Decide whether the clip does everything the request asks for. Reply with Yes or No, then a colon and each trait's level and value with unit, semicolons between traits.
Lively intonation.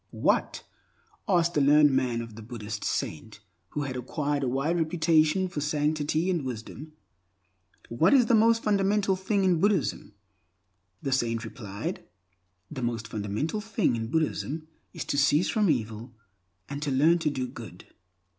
Yes: wide, 6.4 semitones